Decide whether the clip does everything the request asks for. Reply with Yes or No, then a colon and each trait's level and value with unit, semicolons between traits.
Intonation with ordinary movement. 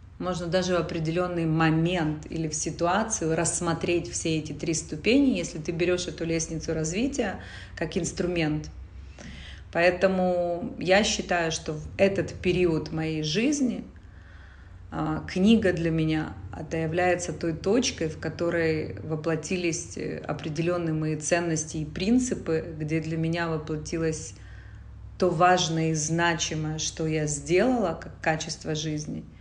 No: narrow, 2.2 semitones